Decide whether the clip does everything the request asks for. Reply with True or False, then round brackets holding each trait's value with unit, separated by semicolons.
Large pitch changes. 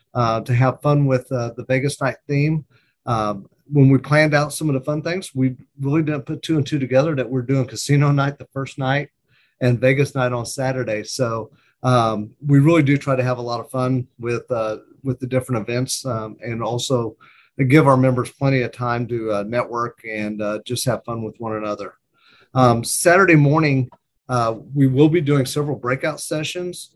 False (3.2 semitones)